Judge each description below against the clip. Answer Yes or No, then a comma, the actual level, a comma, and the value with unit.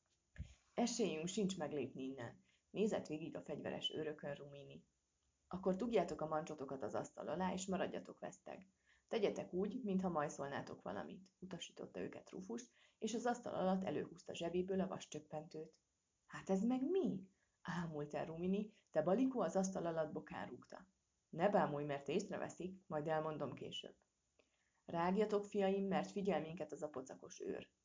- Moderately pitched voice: Yes, medium, 175 Hz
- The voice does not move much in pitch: No, average, 4.8 semitones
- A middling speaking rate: Yes, average, 140 wpm